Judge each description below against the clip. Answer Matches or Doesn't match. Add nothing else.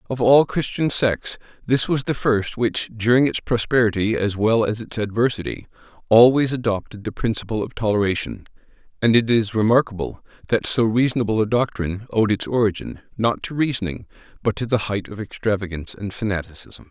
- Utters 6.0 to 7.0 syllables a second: Doesn't match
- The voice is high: Doesn't match